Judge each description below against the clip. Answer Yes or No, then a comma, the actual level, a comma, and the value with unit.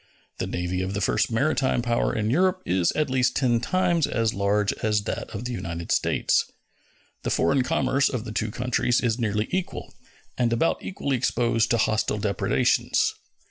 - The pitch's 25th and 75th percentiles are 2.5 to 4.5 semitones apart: Yes, average, 3.8 semitones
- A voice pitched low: Yes, low, 120 Hz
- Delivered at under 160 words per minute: No, average, 175 wpm